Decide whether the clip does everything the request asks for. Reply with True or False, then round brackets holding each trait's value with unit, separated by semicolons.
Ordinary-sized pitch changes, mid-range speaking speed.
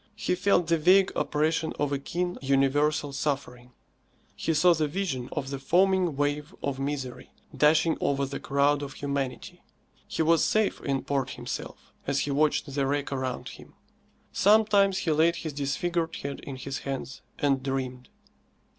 True (3.3 semitones; 160 wpm)